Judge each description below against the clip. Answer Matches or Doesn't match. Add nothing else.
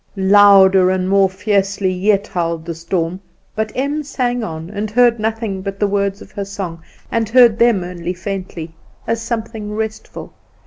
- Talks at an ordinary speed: Matches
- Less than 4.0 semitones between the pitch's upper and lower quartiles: Matches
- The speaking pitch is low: Doesn't match